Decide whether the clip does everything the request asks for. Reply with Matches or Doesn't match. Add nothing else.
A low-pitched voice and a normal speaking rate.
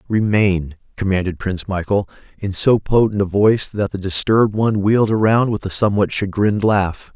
Matches